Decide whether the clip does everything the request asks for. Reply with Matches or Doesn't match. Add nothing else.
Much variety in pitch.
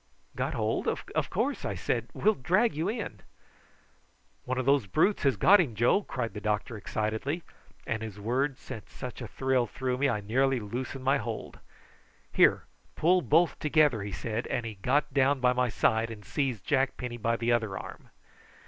Doesn't match